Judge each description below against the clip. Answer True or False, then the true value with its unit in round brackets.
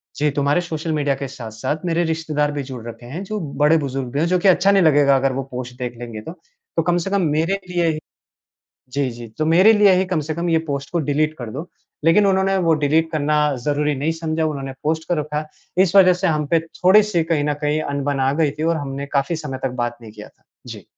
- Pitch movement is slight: False (3.4 semitones)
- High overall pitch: False (150 Hz)